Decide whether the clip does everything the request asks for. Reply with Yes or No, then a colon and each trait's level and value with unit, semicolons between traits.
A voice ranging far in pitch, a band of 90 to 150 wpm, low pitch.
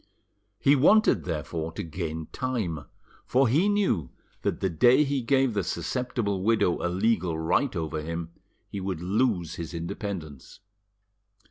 Yes: wide, 7.2 semitones; average, 140 wpm; very low, 95 Hz